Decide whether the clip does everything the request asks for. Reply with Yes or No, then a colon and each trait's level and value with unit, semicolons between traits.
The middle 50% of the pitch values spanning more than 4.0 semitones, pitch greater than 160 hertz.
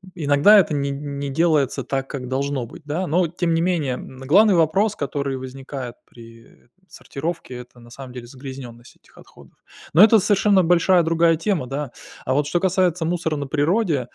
No: average, 4.7 semitones; medium, 150 Hz